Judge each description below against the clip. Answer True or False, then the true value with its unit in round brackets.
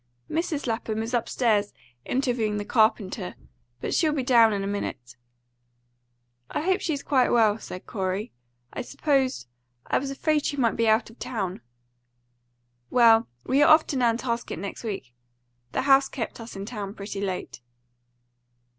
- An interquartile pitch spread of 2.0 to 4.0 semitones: False (4.7 semitones)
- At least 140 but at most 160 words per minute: True (155 wpm)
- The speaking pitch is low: False (230 Hz)